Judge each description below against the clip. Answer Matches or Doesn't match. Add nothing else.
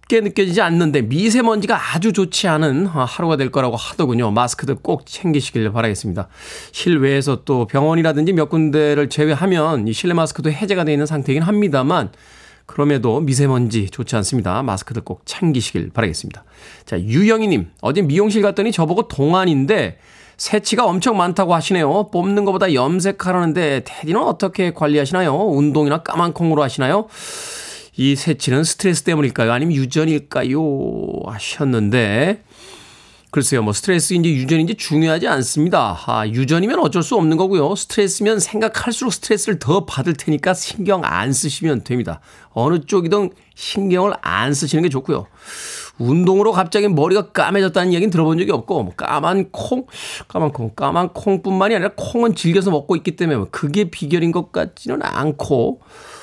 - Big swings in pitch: Matches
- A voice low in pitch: Doesn't match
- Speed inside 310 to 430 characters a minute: Matches